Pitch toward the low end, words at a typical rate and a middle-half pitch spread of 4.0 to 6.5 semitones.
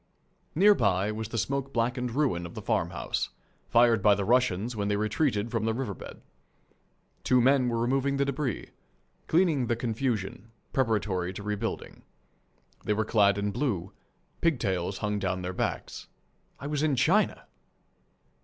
Yes: low, 115 Hz; average, 150 wpm; average, 4.7 semitones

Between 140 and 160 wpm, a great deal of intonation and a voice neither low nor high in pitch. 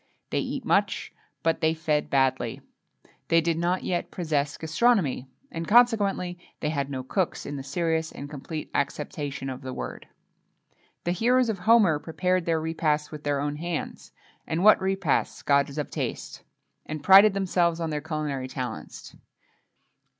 No: average, 155 wpm; average, 3.9 semitones; medium, 160 Hz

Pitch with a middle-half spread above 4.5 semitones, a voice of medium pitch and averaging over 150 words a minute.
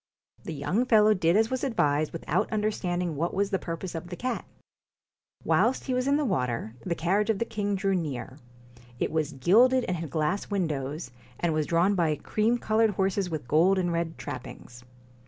Yes: average, 5.2 semitones; medium, 180 Hz; average, 190 wpm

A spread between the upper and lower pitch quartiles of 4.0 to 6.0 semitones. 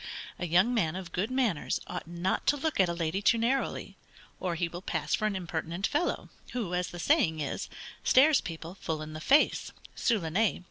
Yes: wide, 5.5 semitones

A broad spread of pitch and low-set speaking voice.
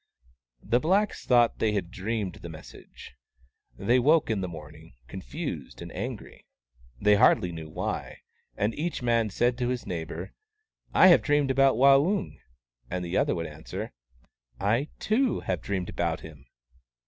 Yes: wide, 7.8 semitones; low, 105 Hz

